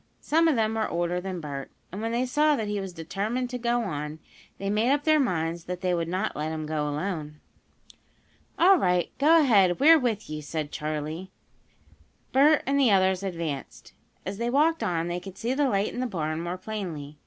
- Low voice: No, high, 190 Hz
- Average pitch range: No, wide, 7.0 semitones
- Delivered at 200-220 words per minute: Yes, fast, 205 wpm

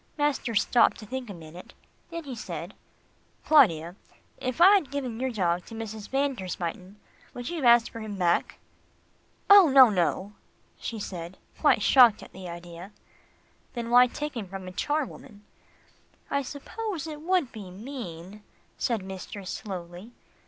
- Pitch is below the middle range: No, high, 225 Hz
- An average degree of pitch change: No, wide, 6.5 semitones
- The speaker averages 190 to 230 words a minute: No, average, 160 wpm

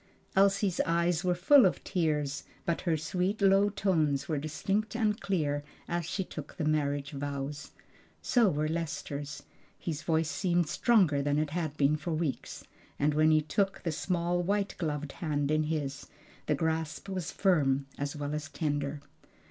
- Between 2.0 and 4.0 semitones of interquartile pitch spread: Yes, average, 3.7 semitones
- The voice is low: No, medium, 155 Hz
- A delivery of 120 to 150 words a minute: No, average, 165 wpm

